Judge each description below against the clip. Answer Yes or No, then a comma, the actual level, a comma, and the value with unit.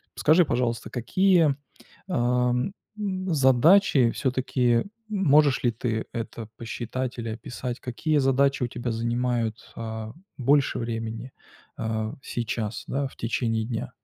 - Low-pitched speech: Yes, low, 125 Hz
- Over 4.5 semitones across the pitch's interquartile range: No, average, 3.1 semitones